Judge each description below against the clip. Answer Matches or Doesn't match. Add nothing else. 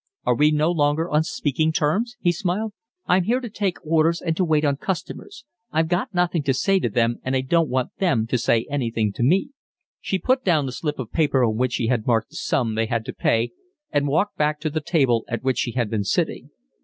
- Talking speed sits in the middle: Doesn't match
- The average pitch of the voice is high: Doesn't match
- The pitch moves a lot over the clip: Matches